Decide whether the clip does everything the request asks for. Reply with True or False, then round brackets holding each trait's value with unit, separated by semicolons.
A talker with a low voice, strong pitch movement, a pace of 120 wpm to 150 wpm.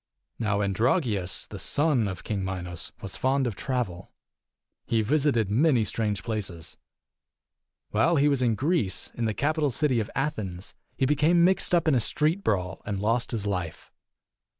False (115 Hz; 6.5 semitones; 165 wpm)